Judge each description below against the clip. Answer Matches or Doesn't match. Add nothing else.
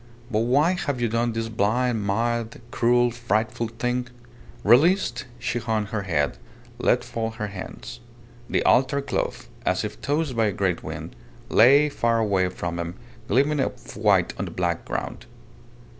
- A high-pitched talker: Doesn't match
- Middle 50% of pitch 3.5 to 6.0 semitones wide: Doesn't match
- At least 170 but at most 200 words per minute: Doesn't match